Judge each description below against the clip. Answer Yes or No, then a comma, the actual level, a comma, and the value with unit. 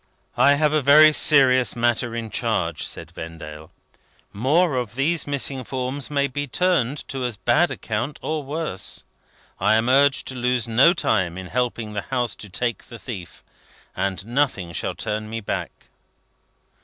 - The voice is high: No, low, 125 Hz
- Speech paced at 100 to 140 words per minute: No, average, 160 wpm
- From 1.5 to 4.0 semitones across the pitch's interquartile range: No, average, 4.6 semitones